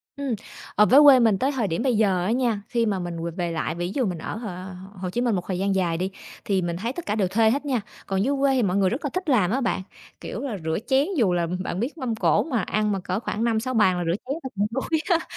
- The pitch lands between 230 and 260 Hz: No, high, 215 Hz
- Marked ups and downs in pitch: Yes, wide, 5.7 semitones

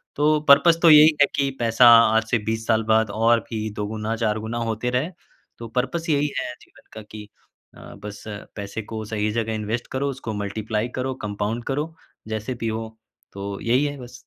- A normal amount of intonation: Yes, average, 3.2 semitones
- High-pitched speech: No, low, 115 Hz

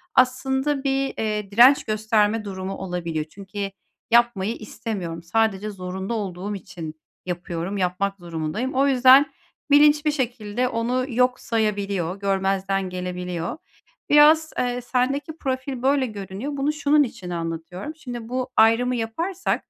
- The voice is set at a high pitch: Yes, high, 220 Hz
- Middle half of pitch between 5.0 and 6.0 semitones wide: Yes, wide, 5.4 semitones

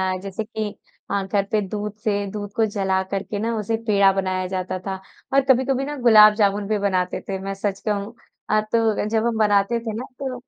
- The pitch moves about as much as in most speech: No, narrow, 2.2 semitones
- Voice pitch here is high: Yes, high, 210 Hz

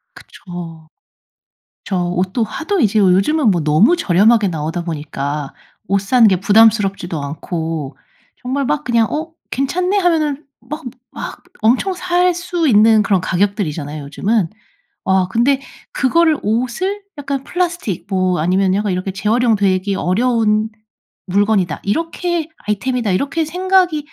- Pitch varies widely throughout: Yes, wide, 7.9 semitones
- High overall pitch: Yes, high, 215 Hz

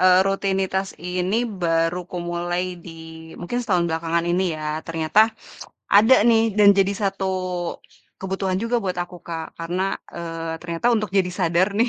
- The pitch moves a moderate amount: No, narrow, 2.3 semitones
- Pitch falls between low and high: Yes, medium, 180 Hz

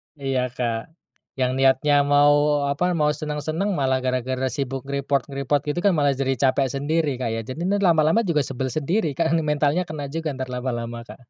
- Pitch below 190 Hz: Yes, medium, 140 Hz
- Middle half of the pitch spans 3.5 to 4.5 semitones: No, average, 2.9 semitones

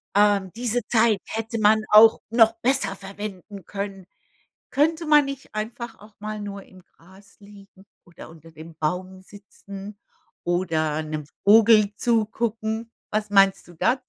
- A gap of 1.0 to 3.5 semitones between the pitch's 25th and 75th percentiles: Yes, average, 2.9 semitones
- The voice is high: Yes, high, 205 Hz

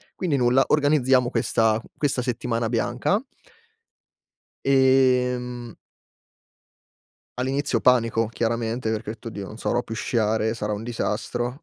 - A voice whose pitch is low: Yes, low, 120 Hz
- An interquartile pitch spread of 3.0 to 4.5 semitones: No, narrow, 2.4 semitones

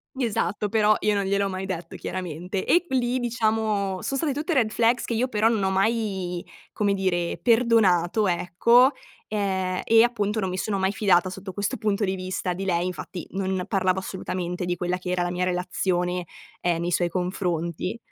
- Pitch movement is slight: No, average, 3.3 semitones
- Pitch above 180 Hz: Yes, high, 190 Hz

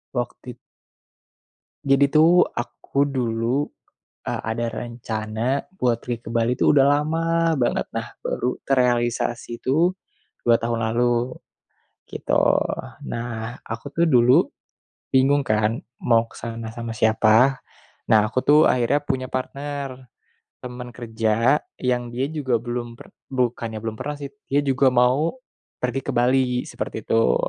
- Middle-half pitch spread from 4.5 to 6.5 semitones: No, average, 2.8 semitones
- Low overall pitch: Yes, low, 125 Hz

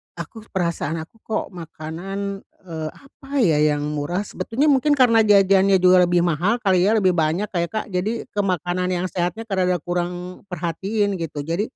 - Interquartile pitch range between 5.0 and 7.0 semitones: No, average, 3.1 semitones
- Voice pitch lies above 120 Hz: Yes, medium, 185 Hz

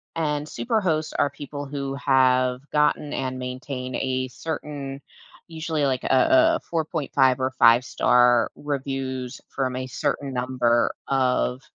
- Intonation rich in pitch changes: No, narrow, 2.6 semitones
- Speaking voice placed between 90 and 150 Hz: Yes, low, 135 Hz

